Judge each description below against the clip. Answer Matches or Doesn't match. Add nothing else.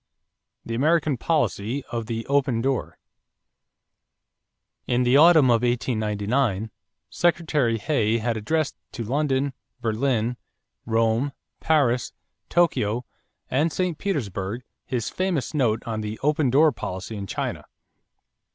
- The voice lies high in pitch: Doesn't match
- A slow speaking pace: Matches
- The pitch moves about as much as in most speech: Matches